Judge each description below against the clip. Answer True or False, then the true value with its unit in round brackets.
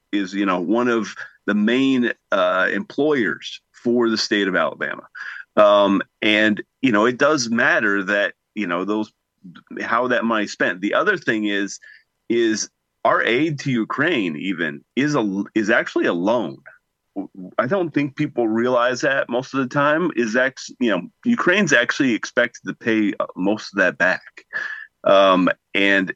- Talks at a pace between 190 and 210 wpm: False (160 wpm)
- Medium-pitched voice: False (115 Hz)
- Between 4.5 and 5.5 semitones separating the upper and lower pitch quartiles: True (4.9 semitones)